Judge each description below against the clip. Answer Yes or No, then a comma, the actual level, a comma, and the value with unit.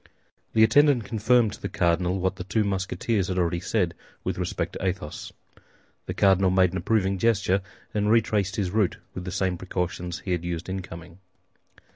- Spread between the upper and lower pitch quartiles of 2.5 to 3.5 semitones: Yes, average, 2.8 semitones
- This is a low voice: Yes, very low, 95 Hz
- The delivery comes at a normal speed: Yes, average, 180 wpm